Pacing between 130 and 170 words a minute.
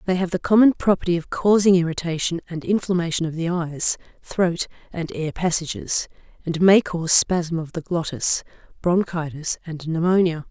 Yes: average, 155 wpm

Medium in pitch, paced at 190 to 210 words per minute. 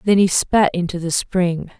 Yes: medium, 180 Hz; average, 200 wpm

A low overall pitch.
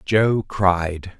Yes: very low, 95 Hz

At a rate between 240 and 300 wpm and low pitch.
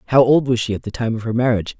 No: fast, 335 wpm; low, 120 Hz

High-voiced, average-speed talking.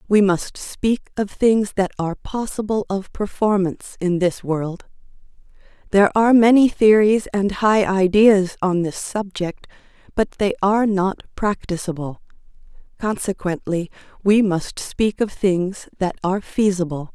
No: high, 195 Hz; slow, 130 wpm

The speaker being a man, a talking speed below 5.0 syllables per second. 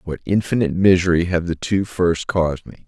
No: male; 5.7 syllables/s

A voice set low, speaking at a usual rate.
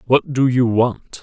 Yes: low, 125 Hz; average, 195 wpm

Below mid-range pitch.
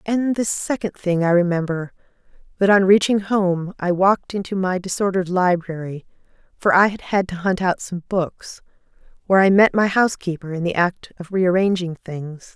No: medium, 185 Hz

